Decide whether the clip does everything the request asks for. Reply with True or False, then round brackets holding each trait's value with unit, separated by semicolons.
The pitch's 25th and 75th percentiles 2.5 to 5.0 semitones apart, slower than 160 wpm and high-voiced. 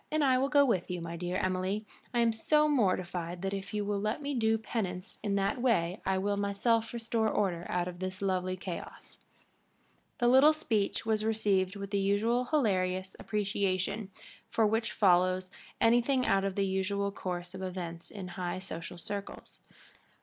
False (3.3 semitones; 170 wpm; 200 Hz)